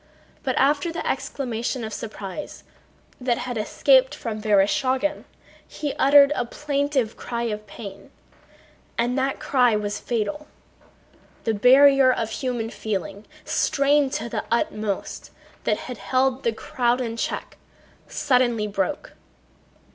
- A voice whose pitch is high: Yes, high, 245 Hz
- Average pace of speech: No, slow, 125 wpm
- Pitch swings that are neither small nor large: Yes, average, 3.9 semitones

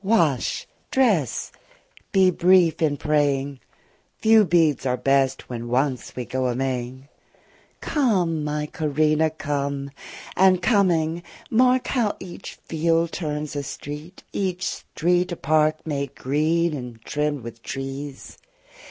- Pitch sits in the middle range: Yes, medium, 150 Hz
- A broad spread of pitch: No, average, 4.1 semitones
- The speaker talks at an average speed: No, slow, 125 wpm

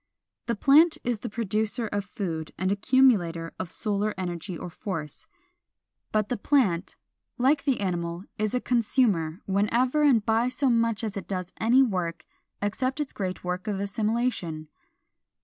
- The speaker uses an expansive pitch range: No, average, 4.9 semitones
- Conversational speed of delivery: Yes, average, 150 wpm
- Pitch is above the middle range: Yes, high, 210 Hz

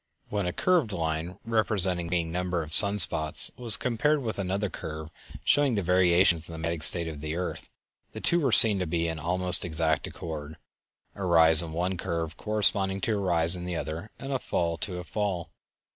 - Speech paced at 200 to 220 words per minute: Yes, fast, 205 wpm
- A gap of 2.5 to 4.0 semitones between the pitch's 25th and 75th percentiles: Yes, average, 3.6 semitones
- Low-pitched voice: Yes, very low, 90 Hz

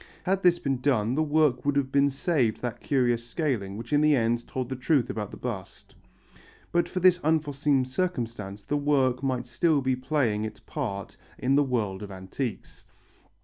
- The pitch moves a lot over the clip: No, average, 3.9 semitones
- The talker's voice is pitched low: Yes, low, 130 Hz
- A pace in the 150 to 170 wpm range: No, average, 185 wpm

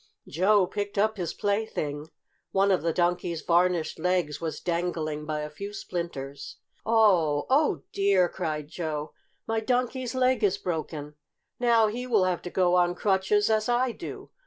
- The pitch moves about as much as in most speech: Yes, average, 4.9 semitones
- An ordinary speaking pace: Yes, average, 160 wpm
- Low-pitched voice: No, medium, 180 Hz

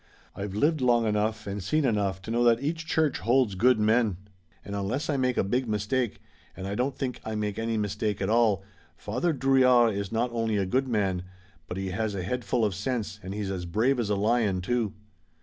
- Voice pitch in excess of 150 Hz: No, low, 110 Hz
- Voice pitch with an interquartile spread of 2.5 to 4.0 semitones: Yes, average, 3.7 semitones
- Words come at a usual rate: No, fast, 220 wpm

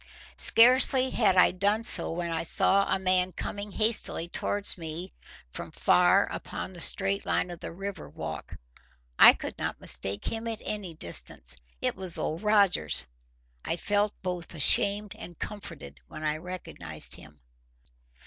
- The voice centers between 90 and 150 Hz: No, medium, 185 Hz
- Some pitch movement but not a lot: Yes, average, 4.2 semitones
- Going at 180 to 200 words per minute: No, average, 150 wpm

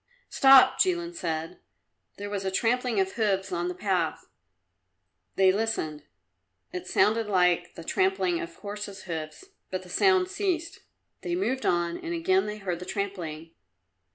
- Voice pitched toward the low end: No, high, 195 Hz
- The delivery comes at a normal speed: Yes, average, 150 wpm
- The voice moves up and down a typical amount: No, wide, 6.5 semitones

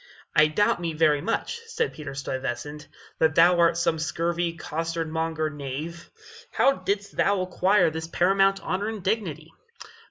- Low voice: No, medium, 165 Hz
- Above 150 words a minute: No, average, 140 wpm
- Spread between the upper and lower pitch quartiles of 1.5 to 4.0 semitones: Yes, average, 3.4 semitones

